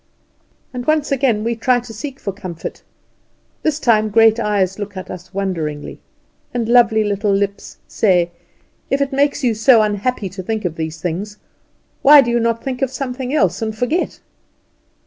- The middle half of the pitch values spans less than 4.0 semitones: No, average, 4.3 semitones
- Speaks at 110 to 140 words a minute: No, average, 170 wpm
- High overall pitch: Yes, high, 220 Hz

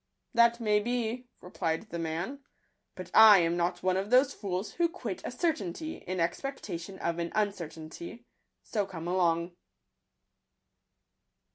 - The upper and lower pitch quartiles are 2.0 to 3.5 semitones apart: No, wide, 5.5 semitones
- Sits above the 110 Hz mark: Yes, high, 190 Hz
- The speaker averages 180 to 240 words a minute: No, average, 155 wpm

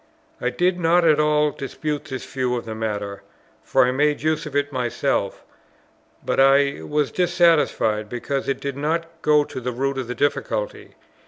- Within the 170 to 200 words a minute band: Yes, average, 175 wpm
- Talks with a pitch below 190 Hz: Yes, medium, 140 Hz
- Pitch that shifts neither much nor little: Yes, average, 3.3 semitones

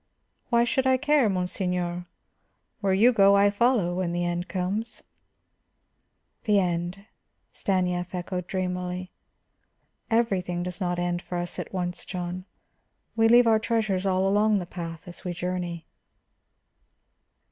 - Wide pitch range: No, average, 2.8 semitones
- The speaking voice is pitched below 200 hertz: Yes, medium, 185 Hz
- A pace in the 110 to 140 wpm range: Yes, slow, 135 wpm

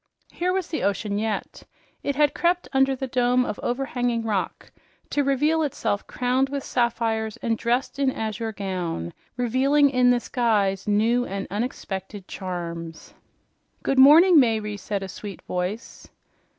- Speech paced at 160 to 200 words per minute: No, average, 145 wpm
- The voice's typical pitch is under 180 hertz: No, high, 235 Hz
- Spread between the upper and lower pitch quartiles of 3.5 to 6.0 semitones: Yes, average, 4.7 semitones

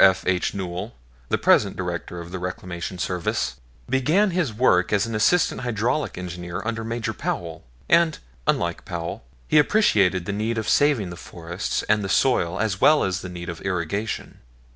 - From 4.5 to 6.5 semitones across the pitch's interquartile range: Yes, average, 4.8 semitones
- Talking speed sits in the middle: Yes, average, 170 wpm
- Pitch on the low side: Yes, low, 100 Hz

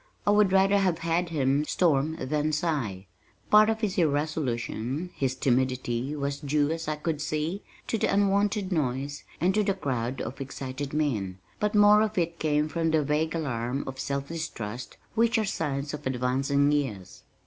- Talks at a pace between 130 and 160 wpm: No, average, 170 wpm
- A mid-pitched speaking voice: Yes, medium, 150 Hz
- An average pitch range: Yes, average, 4.7 semitones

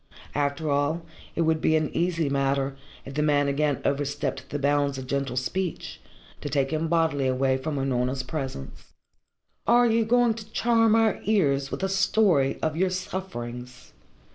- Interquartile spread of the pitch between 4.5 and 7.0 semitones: Yes, average, 5.0 semitones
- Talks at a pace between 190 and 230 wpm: No, average, 165 wpm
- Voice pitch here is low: No, medium, 145 Hz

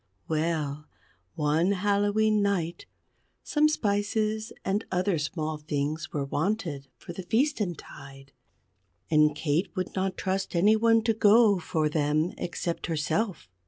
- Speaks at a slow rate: Yes, slow, 125 wpm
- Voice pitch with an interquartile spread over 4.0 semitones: Yes, average, 5.1 semitones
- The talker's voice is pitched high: No, medium, 180 Hz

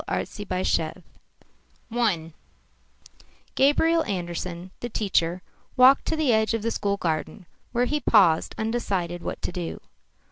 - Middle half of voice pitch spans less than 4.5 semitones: No, wide, 5.5 semitones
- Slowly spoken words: Yes, slow, 120 wpm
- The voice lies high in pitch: Yes, high, 200 Hz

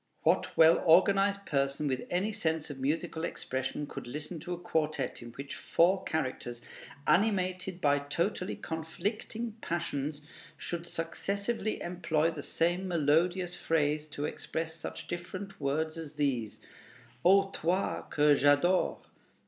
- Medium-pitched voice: Yes, medium, 165 Hz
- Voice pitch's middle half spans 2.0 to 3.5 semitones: No, average, 3.9 semitones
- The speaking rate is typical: No, slow, 130 wpm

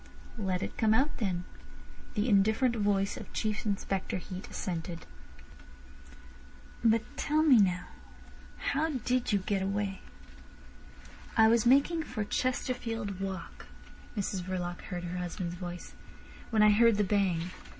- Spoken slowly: Yes, slow, 130 wpm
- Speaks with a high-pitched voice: Yes, high, 205 Hz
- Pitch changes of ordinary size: Yes, average, 3.8 semitones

